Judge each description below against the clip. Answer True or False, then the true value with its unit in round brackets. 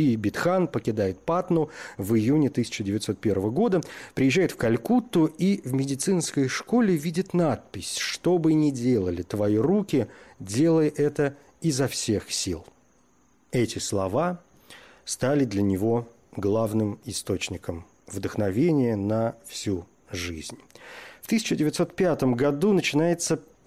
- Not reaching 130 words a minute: True (110 wpm)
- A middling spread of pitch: False (7.5 semitones)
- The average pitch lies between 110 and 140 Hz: True (135 Hz)